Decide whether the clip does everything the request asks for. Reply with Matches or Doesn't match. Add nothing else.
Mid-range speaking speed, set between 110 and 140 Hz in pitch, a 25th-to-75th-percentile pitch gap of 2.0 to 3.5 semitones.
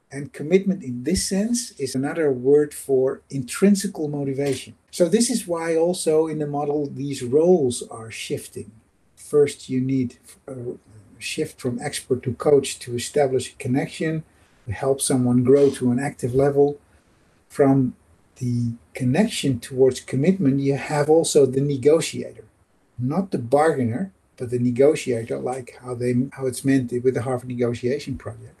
Matches